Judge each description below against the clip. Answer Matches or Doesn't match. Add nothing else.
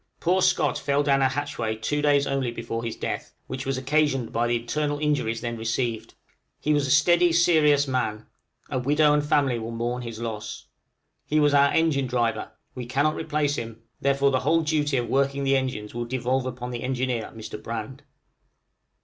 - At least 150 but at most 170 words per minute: Doesn't match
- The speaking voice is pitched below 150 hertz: Matches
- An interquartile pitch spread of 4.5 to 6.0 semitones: Doesn't match